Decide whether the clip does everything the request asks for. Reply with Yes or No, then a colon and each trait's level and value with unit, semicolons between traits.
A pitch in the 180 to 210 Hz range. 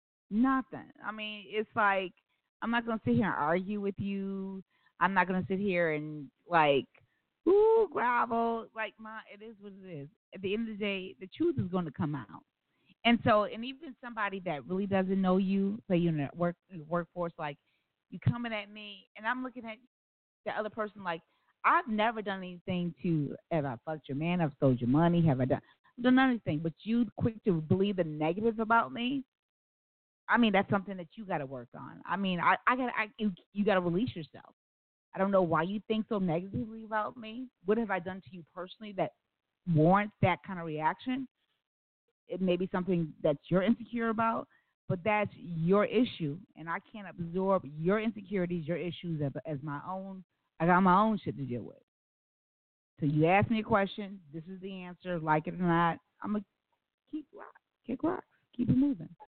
Yes: high, 190 Hz